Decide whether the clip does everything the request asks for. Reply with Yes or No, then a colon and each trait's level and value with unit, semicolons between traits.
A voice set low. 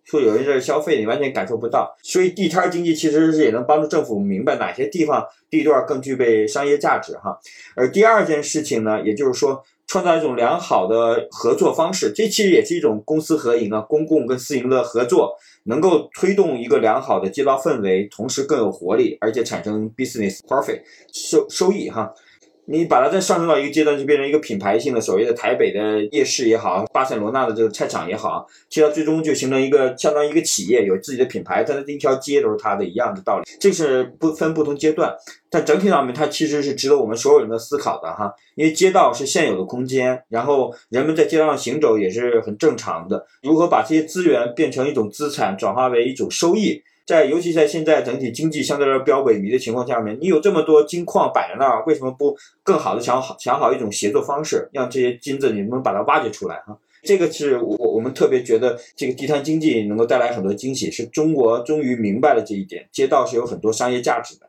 No: medium, 150 Hz